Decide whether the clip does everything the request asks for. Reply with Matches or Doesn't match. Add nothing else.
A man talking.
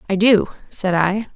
Doesn't match